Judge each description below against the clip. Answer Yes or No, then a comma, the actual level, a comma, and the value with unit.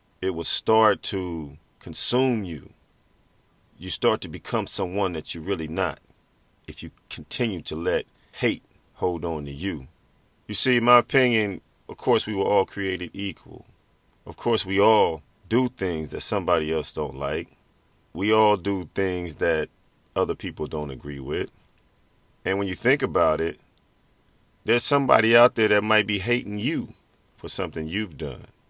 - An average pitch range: Yes, average, 5.0 semitones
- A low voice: Yes, very low, 95 Hz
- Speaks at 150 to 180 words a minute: Yes, average, 160 wpm